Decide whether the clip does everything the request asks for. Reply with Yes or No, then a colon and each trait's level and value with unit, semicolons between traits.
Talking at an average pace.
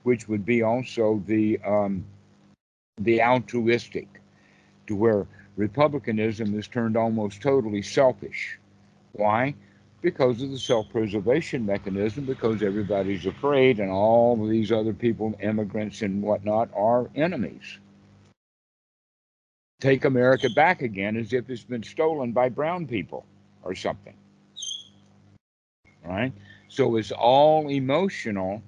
No: slow, 115 wpm